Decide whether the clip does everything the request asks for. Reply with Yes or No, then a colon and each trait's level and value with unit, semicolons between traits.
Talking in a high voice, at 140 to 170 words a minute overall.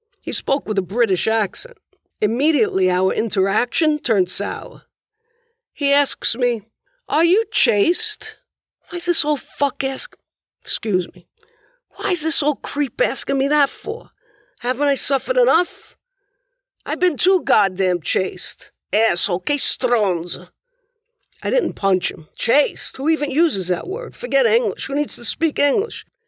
Yes: very high, 295 Hz; average, 145 wpm